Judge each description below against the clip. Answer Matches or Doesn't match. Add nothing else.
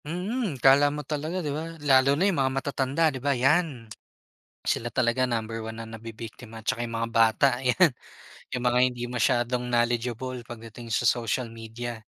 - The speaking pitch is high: Doesn't match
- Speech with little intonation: Doesn't match